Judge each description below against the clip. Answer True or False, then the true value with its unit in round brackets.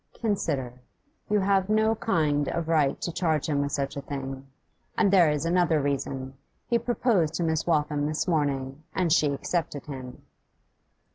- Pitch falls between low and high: True (155 Hz)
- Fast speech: False (160 wpm)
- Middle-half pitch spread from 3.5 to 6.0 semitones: True (4.0 semitones)